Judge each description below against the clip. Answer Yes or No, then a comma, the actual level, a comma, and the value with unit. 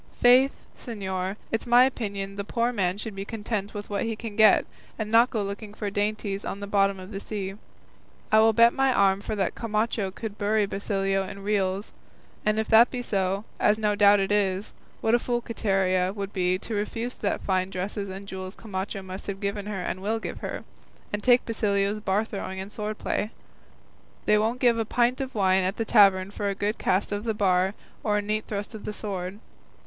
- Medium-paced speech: No, fast, 210 wpm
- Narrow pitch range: Yes, narrow, 2.1 semitones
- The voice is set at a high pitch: Yes, high, 205 Hz